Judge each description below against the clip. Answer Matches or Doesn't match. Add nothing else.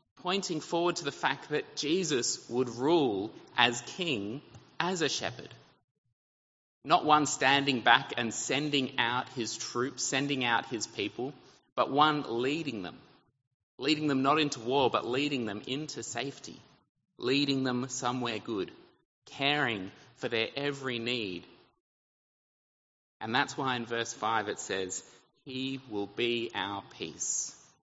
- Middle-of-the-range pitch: Doesn't match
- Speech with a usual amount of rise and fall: Matches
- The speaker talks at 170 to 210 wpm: Doesn't match